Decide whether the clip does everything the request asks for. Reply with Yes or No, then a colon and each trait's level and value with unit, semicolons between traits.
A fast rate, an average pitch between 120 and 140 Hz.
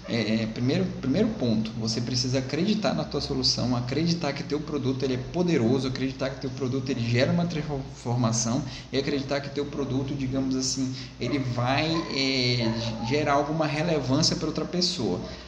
No: average, 160 wpm; low, 135 Hz